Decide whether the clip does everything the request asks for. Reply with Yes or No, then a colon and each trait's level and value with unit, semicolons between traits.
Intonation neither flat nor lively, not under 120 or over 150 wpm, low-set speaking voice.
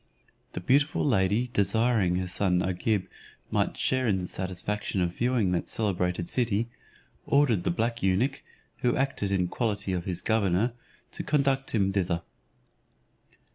Yes: average, 4.7 semitones; average, 140 wpm; low, 100 Hz